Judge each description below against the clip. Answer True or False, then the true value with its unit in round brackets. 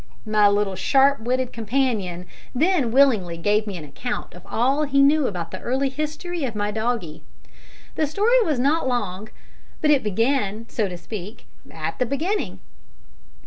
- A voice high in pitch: True (240 Hz)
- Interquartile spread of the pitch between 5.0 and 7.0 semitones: True (5.3 semitones)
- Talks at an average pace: True (160 wpm)